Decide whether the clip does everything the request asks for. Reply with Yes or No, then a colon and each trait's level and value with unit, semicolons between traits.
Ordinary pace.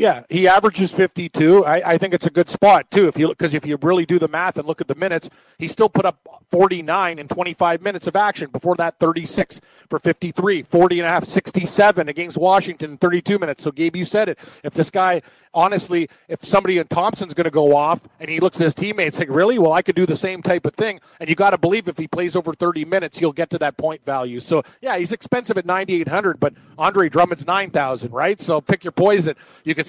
No: fast, 240 wpm